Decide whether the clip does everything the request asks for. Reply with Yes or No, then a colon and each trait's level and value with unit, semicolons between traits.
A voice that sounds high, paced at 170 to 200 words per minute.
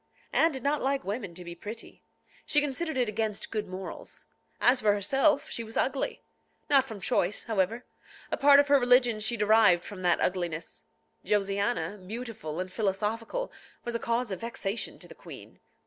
Yes: high, 220 Hz; average, 175 wpm